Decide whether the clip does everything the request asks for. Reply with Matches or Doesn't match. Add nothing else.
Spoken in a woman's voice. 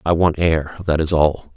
Doesn't match